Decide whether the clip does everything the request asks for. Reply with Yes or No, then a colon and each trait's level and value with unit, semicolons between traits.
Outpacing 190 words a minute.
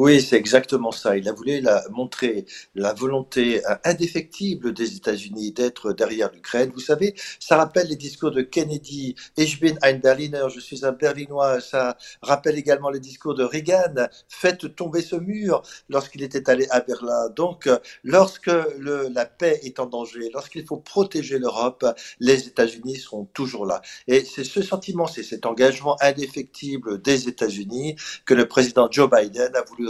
No: average, 165 wpm